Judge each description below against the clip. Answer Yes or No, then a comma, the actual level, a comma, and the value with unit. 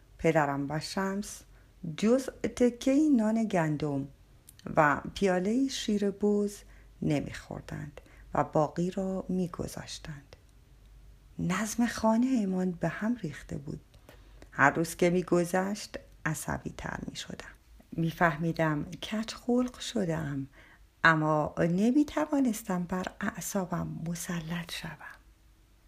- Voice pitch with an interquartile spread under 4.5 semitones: No, average, 5.3 semitones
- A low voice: No, medium, 180 Hz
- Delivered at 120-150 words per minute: No, slow, 105 wpm